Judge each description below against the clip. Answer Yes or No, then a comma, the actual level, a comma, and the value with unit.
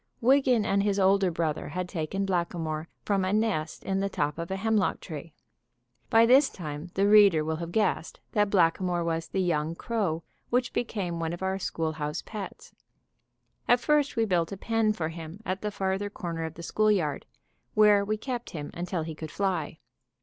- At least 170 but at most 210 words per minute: Yes, average, 185 wpm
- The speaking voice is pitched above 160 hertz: Yes, high, 190 Hz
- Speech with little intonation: No, average, 4.2 semitones